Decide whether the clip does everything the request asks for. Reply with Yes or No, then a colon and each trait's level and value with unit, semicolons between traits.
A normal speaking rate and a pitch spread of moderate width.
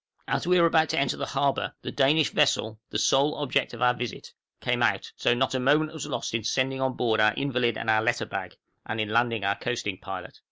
No: fast, 235 wpm; average, 3.9 semitones